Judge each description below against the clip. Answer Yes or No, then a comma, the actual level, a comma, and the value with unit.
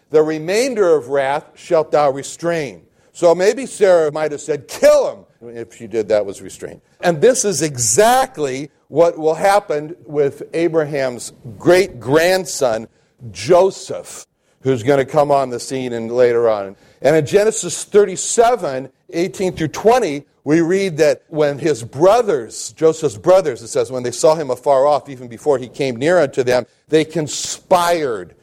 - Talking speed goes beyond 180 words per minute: No, average, 155 wpm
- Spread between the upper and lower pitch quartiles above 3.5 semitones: Yes, average, 5.3 semitones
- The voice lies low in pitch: No, medium, 155 Hz